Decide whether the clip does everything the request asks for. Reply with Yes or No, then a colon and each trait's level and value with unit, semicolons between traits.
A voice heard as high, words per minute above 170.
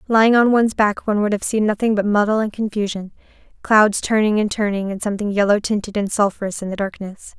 Yes: high, 210 Hz; fast, 205 wpm